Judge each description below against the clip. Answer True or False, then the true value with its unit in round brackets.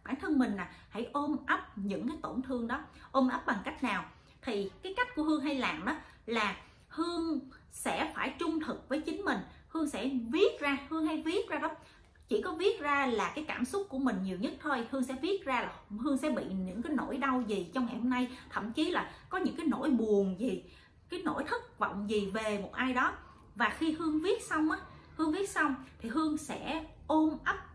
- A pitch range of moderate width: True (4.1 semitones)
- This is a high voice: True (285 Hz)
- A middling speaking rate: True (225 wpm)